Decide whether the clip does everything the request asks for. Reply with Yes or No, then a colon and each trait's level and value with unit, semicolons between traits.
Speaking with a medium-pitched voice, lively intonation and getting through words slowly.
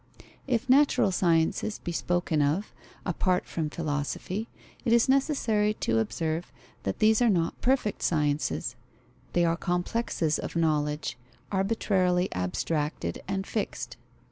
Yes: medium, 175 Hz; wide, 5.7 semitones; slow, 120 wpm